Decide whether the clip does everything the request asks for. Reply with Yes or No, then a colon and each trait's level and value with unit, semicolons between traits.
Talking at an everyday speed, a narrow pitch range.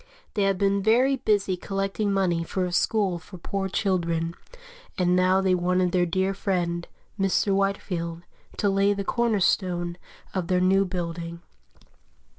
Yes: average, 150 wpm; narrow, 2.0 semitones